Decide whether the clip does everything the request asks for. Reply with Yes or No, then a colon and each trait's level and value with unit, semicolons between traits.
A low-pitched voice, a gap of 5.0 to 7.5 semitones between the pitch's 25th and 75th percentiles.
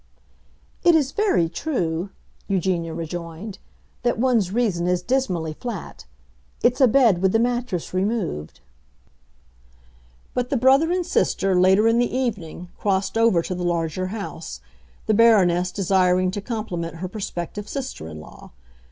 No: high, 195 Hz; wide, 5.4 semitones